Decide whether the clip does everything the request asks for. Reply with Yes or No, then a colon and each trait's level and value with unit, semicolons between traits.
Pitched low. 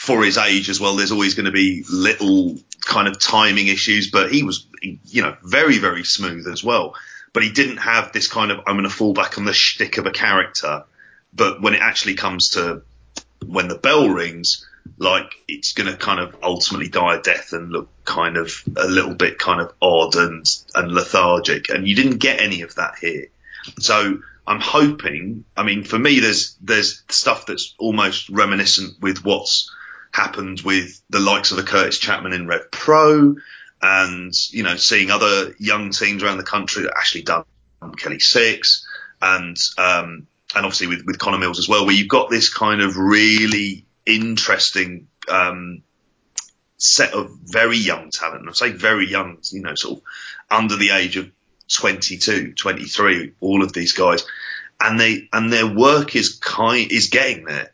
Yes: low, 100 Hz